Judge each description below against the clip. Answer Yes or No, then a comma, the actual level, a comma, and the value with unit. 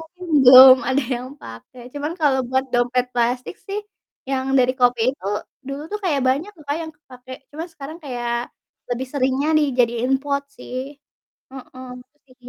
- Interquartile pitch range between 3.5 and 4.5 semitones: No, average, 2.7 semitones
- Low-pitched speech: No, very high, 260 Hz